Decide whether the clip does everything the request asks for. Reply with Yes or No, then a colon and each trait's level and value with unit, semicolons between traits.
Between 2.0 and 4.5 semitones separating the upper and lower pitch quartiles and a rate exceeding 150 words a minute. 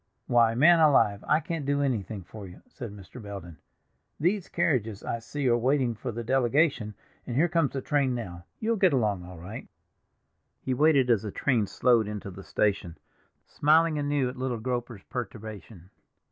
No: wide, 5.5 semitones; average, 175 wpm